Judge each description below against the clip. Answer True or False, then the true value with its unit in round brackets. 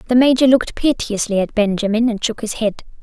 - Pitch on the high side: True (225 Hz)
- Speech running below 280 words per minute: True (200 wpm)